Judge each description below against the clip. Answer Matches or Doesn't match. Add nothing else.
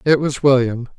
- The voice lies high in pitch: Doesn't match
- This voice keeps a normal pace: Matches